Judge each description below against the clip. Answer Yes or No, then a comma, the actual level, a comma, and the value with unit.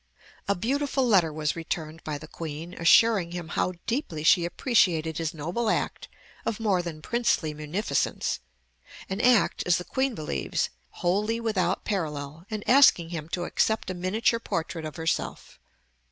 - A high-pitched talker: No, medium, 175 Hz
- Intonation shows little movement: No, wide, 5.4 semitones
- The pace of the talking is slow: No, average, 155 wpm